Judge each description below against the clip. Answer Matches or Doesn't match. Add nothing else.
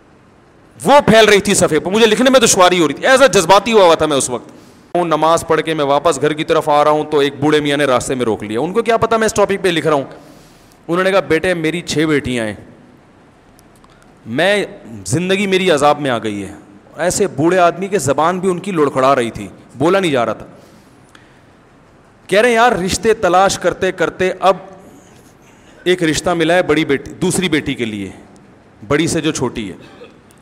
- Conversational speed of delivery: Doesn't match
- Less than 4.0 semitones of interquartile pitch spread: Doesn't match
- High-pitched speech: Doesn't match